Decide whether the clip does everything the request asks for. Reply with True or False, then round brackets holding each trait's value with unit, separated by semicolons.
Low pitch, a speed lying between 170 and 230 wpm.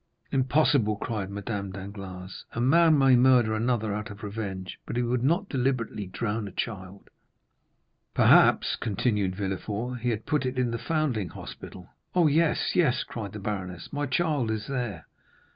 False (115 Hz; 160 wpm)